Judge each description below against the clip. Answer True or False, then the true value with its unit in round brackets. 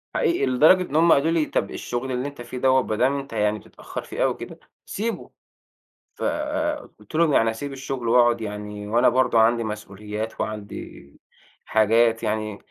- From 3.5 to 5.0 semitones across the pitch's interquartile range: True (4.1 semitones)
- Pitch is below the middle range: True (120 Hz)